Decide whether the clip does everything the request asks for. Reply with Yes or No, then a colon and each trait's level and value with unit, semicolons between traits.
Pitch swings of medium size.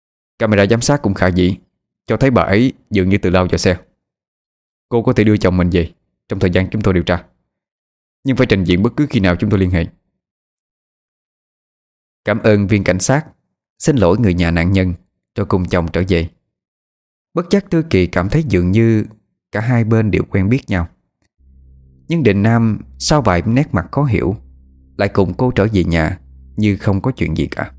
Yes: average, 4.1 semitones